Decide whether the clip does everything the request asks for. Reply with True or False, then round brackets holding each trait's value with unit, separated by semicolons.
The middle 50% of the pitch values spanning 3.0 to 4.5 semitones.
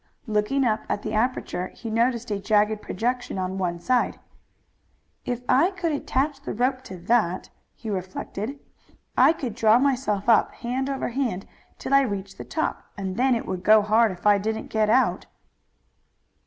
True (4.1 semitones)